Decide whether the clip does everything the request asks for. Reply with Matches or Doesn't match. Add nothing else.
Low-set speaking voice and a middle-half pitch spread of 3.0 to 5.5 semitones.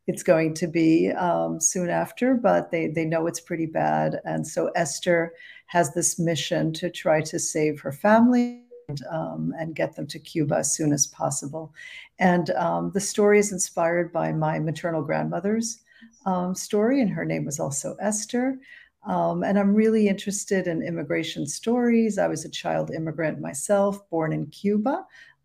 Doesn't match